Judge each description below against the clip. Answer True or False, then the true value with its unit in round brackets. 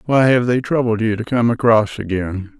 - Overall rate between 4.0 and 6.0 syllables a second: True (4.9 syllables/s)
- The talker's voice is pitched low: True (115 Hz)